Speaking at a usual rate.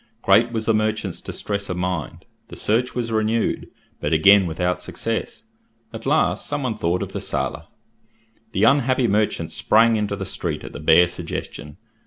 Yes: average, 170 wpm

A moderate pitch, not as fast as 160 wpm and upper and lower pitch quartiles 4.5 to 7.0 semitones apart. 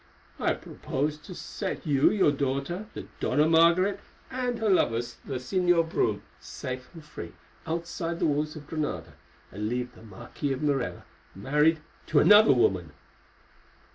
Yes: medium, 150 Hz; average, 150 wpm; average, 4.8 semitones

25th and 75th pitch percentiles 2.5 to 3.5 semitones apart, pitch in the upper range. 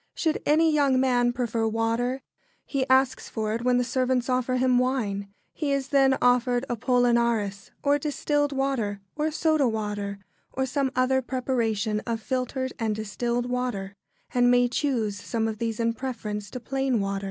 Yes: average, 2.9 semitones; high, 245 Hz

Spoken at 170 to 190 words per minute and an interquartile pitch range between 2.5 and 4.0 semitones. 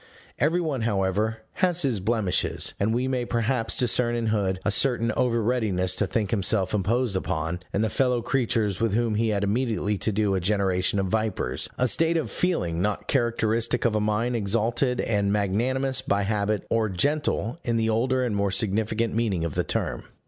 Yes: average, 185 wpm; average, 3.2 semitones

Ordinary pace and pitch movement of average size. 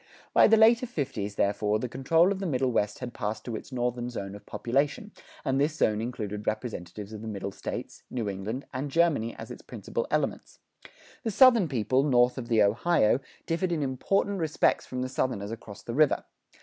No: average, 190 wpm; wide, 6.2 semitones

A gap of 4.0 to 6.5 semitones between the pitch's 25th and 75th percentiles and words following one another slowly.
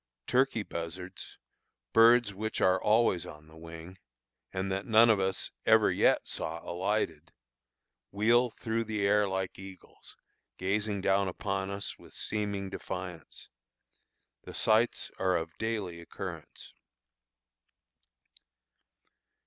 No: average, 3.0 semitones; slow, 115 wpm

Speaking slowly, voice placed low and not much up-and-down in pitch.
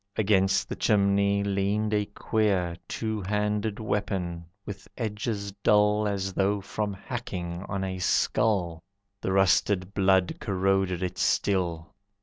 Yes: slow, 125 wpm; low, 100 Hz; narrow, 1.8 semitones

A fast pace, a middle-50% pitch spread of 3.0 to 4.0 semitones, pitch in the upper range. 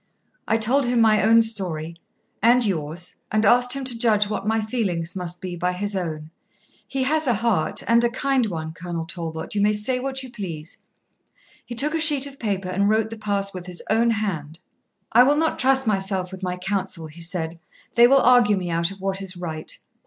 No: fast, 210 wpm; average, 5.0 semitones; high, 205 Hz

